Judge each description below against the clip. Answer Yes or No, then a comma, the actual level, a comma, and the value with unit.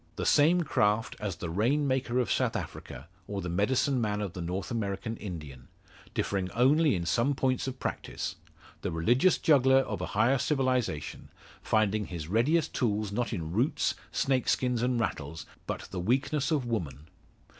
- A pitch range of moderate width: No, wide, 5.8 semitones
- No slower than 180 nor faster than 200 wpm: No, average, 165 wpm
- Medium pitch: No, low, 115 Hz